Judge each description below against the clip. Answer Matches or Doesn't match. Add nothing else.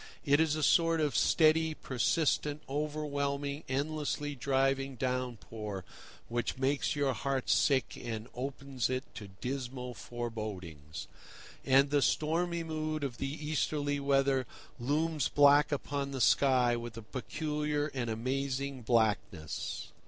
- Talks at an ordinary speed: Doesn't match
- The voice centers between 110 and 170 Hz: Matches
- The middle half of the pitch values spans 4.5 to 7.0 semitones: Doesn't match